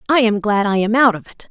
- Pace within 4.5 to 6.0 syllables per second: No, 6.2 syllables/s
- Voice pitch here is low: No, high, 220 Hz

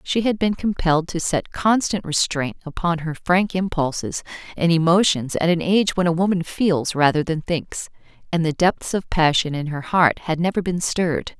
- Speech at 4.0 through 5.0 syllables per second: Yes, 4.9 syllables/s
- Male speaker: No, female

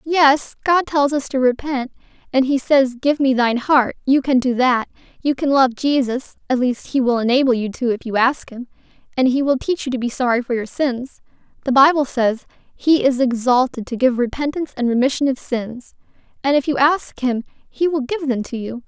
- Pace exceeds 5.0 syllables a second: Yes, 5.2 syllables/s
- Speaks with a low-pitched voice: No, very high, 260 Hz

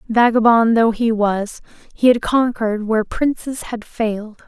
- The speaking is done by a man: No, female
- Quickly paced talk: No, average, 150 wpm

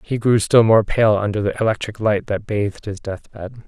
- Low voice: Yes, low, 105 Hz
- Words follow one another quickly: Yes, fast, 210 wpm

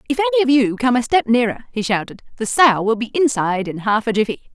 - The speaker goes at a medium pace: No, fast, 250 wpm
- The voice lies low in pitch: No, high, 240 Hz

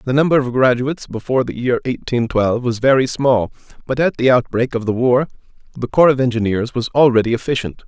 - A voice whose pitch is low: Yes, low, 125 Hz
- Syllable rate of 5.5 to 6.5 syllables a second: Yes, 6.1 syllables/s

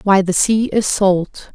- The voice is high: Yes, high, 195 Hz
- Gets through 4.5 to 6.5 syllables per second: No, 3.5 syllables/s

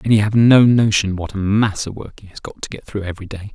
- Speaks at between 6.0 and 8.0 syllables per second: Yes, 6.1 syllables/s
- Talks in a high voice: No, low, 105 Hz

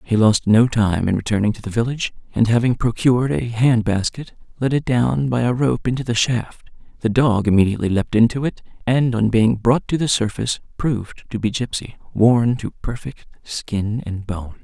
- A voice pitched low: Yes, low, 115 Hz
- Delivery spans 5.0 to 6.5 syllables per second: Yes, 5.1 syllables/s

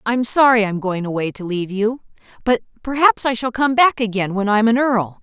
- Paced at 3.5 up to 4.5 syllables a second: No, 5.4 syllables/s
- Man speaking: No, female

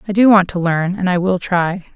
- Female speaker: Yes, female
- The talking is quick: Yes, fast, 275 wpm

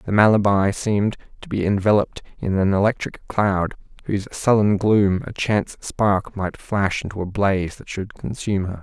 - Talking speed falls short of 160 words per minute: No, average, 170 wpm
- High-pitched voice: No, low, 100 Hz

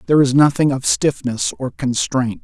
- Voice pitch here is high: No, low, 135 Hz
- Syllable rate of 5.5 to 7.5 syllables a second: No, 5.0 syllables/s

